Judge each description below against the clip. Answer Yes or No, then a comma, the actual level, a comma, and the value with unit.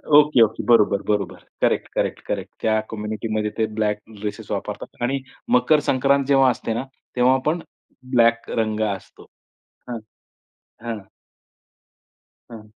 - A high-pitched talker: No, low, 115 Hz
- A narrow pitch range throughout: No, average, 3.3 semitones